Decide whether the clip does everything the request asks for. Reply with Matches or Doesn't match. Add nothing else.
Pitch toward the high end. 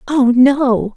Matches